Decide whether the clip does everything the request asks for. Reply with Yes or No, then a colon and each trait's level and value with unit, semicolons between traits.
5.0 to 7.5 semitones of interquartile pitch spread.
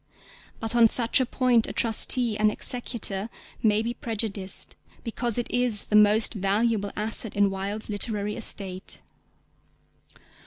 No: narrow, 2.4 semitones